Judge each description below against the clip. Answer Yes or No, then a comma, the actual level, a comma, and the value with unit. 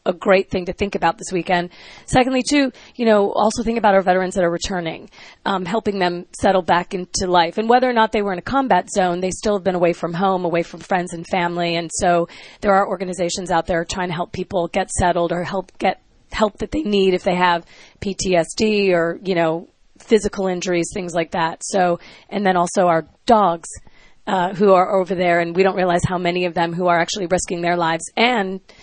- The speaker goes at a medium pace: No, fast, 225 wpm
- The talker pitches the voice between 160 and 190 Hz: Yes, medium, 185 Hz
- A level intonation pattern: Yes, narrow, 2.2 semitones